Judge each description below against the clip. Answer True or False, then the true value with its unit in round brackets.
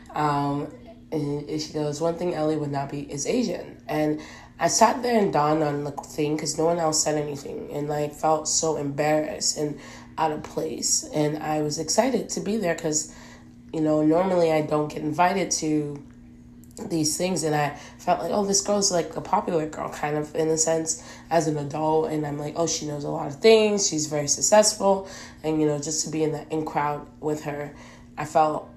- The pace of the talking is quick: True (210 wpm)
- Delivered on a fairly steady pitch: True (1.9 semitones)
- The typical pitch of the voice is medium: True (155 Hz)